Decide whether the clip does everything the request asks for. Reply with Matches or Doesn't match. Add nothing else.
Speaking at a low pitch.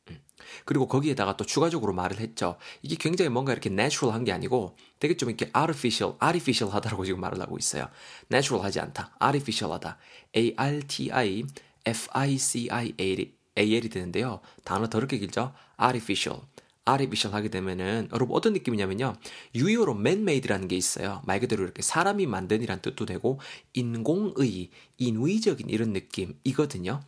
Matches